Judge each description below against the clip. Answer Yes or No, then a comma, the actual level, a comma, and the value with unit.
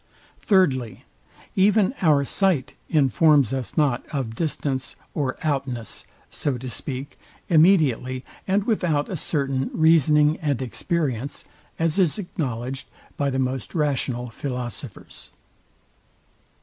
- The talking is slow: Yes, slow, 110 wpm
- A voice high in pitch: No, medium, 140 Hz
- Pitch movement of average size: Yes, average, 3.8 semitones